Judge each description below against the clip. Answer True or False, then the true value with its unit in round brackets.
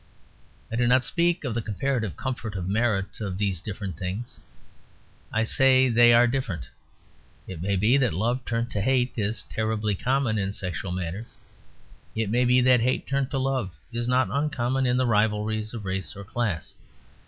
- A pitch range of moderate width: True (4.1 semitones)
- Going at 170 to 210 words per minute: True (175 wpm)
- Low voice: True (115 Hz)